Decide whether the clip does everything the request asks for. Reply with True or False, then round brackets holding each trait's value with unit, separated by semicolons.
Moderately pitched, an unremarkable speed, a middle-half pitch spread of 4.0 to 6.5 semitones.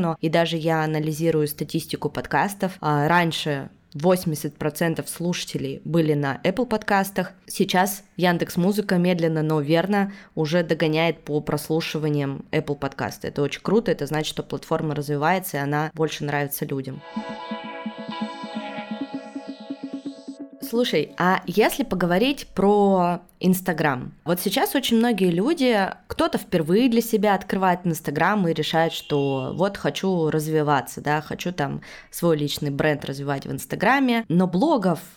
True (170 Hz; 125 wpm; 4.3 semitones)